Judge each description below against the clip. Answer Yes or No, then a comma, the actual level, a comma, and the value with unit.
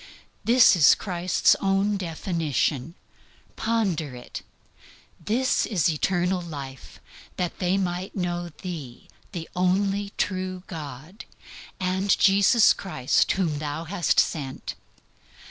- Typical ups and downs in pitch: Yes, average, 3.5 semitones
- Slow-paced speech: Yes, slow, 105 wpm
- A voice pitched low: No, medium, 180 Hz